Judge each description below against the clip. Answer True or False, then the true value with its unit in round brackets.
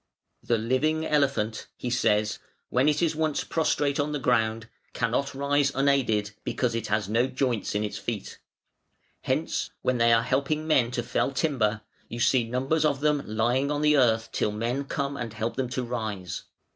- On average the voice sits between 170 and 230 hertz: False (125 Hz)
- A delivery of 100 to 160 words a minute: False (180 wpm)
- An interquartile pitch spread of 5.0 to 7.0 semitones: False (3.9 semitones)